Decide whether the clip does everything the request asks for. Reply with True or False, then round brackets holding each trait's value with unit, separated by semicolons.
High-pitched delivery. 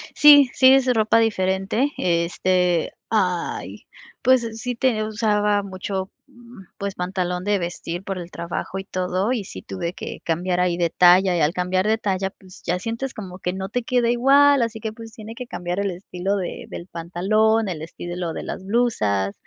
True (195 Hz)